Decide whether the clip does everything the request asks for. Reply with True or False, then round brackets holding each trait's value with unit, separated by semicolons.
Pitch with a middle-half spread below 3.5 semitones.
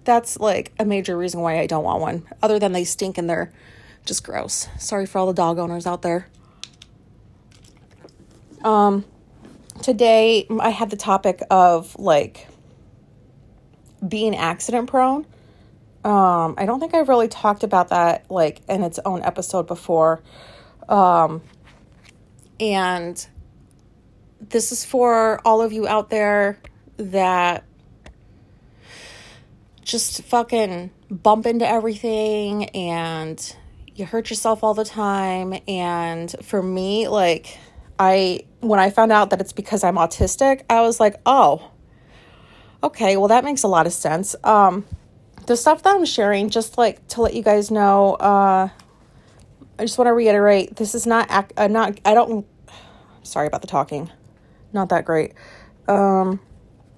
False (4.2 semitones)